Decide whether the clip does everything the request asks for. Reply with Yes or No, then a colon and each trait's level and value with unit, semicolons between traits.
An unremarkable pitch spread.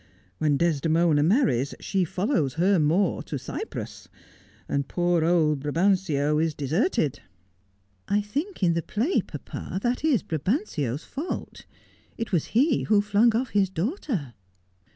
No: wide, 6.4 semitones